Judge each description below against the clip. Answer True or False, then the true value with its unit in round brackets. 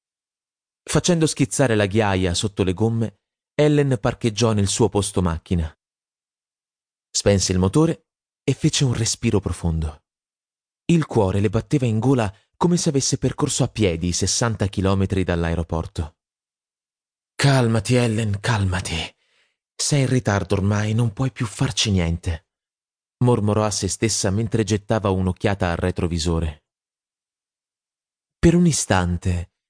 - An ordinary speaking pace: True (125 wpm)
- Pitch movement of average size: True (4.9 semitones)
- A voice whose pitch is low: True (105 Hz)